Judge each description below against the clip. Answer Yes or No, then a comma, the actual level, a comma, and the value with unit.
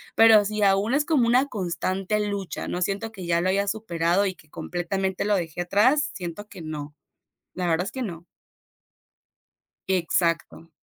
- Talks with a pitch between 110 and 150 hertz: No, high, 190 Hz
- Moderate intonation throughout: Yes, average, 3.4 semitones